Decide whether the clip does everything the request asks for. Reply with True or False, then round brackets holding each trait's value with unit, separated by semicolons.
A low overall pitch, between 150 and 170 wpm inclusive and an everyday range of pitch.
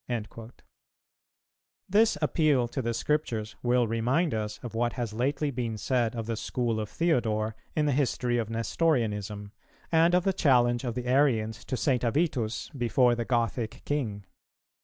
True (120 Hz; 160 wpm; 3.7 semitones)